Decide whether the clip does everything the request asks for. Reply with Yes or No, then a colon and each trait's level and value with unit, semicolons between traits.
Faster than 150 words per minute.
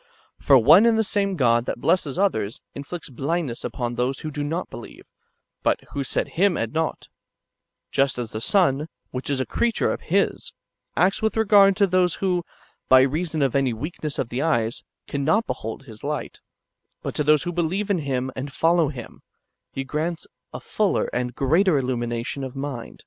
Yes: average, 185 wpm